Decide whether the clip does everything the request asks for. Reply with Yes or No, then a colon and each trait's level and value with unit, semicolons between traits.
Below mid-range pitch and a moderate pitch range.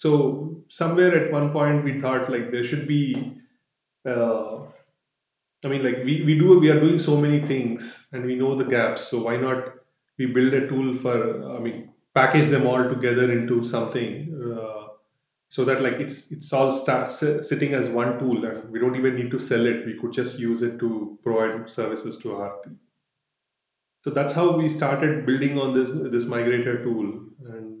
Yes: low, 130 Hz; average, 3.2 semitones